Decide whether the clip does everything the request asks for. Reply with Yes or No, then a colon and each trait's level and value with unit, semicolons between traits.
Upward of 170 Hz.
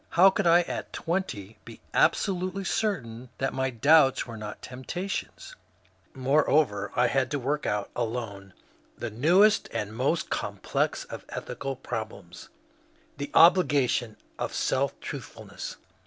No: low, 135 Hz